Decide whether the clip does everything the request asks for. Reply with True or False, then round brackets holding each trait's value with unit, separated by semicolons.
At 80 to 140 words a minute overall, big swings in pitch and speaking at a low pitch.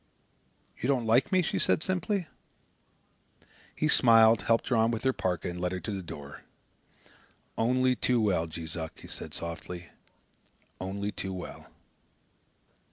False (150 wpm; 5.8 semitones; 110 Hz)